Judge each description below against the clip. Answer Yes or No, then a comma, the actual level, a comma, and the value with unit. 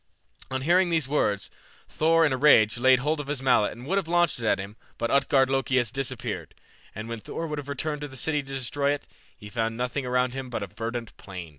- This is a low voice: Yes, low, 130 Hz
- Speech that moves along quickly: Yes, fast, 240 wpm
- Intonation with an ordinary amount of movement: Yes, average, 3.9 semitones